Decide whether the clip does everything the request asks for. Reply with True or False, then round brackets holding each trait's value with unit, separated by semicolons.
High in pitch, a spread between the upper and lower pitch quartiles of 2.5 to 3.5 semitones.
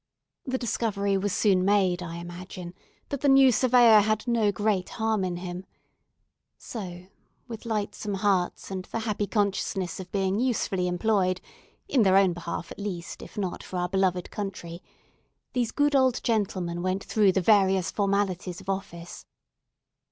True (195 Hz; 3.0 semitones)